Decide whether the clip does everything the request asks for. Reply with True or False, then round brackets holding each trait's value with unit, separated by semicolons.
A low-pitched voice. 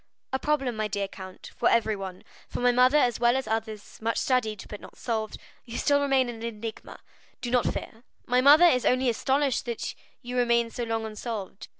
False (235 Hz)